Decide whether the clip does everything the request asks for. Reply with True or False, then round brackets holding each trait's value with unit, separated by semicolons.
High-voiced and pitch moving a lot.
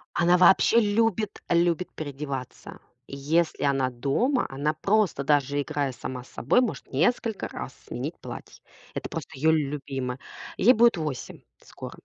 False (155 Hz; 6.2 semitones)